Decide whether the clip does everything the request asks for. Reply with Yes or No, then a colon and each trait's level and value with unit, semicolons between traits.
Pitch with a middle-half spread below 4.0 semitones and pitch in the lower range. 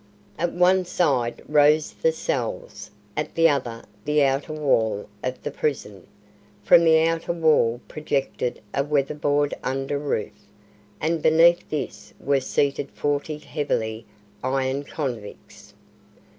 No: average, 3.4 semitones; medium, 145 Hz